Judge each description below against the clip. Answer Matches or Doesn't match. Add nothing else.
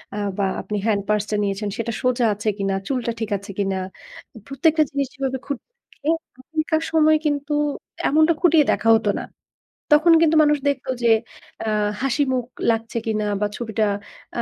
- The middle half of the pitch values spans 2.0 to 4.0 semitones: Doesn't match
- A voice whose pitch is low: Doesn't match